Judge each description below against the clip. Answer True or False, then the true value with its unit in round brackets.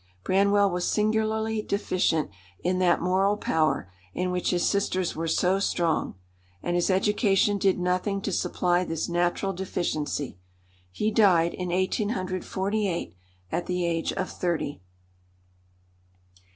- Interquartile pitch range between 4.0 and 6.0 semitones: False (2.4 semitones)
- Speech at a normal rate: False (125 wpm)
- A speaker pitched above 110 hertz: True (185 Hz)